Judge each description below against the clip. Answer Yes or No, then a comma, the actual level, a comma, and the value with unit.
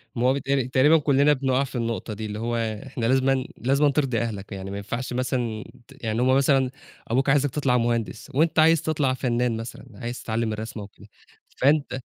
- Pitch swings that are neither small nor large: Yes, average, 3.1 semitones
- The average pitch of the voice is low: Yes, low, 125 Hz